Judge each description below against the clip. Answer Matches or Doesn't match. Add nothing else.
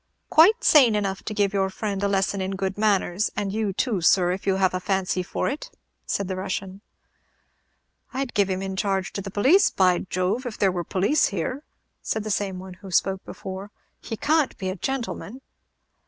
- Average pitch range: Doesn't match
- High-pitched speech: Matches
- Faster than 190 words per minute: Matches